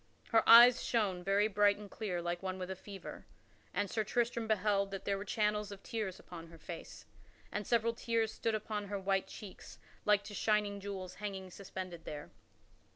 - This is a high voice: Yes, high, 200 Hz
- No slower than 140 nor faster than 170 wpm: No, average, 185 wpm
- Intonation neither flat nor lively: No, narrow, 2.2 semitones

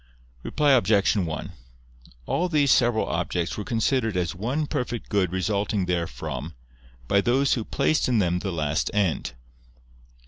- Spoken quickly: No, average, 140 wpm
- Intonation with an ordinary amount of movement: No, wide, 5.7 semitones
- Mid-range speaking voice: No, low, 105 Hz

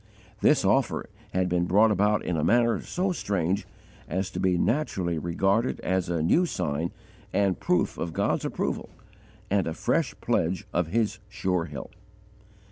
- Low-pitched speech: Yes, very low, 95 Hz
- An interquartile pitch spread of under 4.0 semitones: Yes, average, 3.1 semitones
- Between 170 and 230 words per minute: No, average, 155 wpm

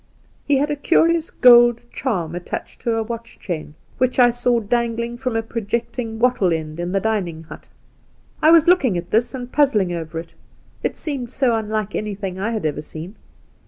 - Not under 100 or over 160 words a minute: No, average, 195 wpm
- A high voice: Yes, high, 225 Hz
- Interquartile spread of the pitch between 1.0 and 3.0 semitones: No, average, 5.1 semitones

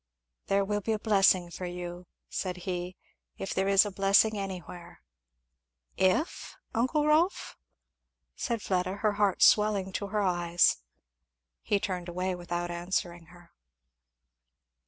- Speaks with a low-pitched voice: No, high, 190 Hz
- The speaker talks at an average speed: No, slow, 130 wpm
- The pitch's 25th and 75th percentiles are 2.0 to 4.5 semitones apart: Yes, average, 2.7 semitones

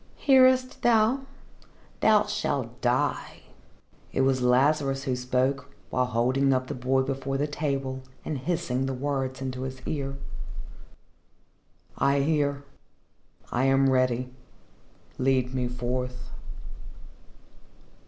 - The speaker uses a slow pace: Yes, slow, 110 wpm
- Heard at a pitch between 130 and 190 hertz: Yes, low, 135 Hz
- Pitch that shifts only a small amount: Yes, narrow, 2.0 semitones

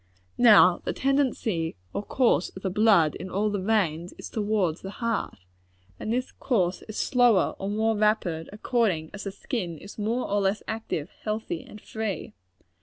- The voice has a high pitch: Yes, high, 205 Hz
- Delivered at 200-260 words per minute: No, average, 170 wpm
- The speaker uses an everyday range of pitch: Yes, average, 3.3 semitones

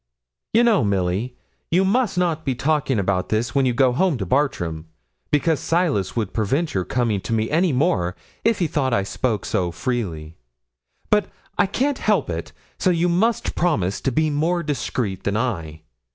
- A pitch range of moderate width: No, wide, 9.0 semitones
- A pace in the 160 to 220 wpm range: Yes, average, 180 wpm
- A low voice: Yes, low, 130 Hz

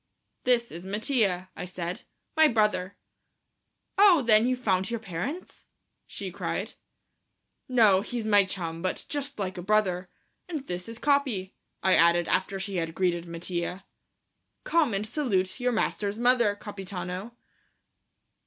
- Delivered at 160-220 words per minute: No, slow, 135 wpm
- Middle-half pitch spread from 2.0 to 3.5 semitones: No, average, 4.7 semitones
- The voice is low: No, high, 200 Hz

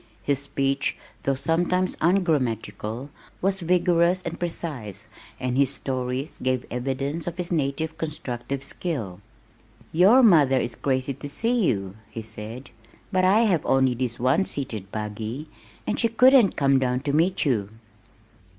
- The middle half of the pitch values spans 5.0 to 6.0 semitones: Yes, wide, 5.5 semitones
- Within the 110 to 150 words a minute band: Yes, average, 140 wpm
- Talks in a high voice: No, medium, 140 Hz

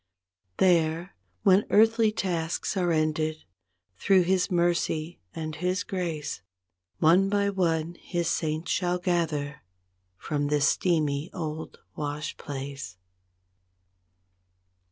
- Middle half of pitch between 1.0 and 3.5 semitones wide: Yes, average, 2.9 semitones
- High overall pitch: No, medium, 165 Hz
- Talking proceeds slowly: Yes, slow, 100 wpm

